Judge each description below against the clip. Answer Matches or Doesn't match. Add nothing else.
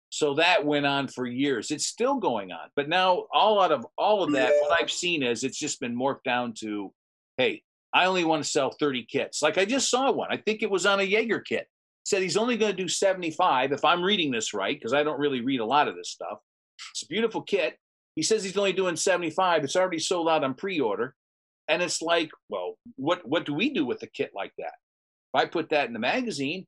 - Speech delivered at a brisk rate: Matches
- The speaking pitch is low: Doesn't match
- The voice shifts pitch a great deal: Matches